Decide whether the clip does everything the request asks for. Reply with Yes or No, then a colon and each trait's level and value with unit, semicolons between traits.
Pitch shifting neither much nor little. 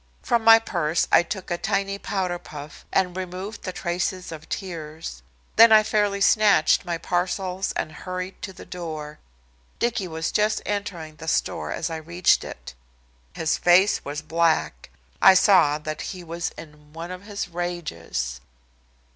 Yes: average, 3.5 semitones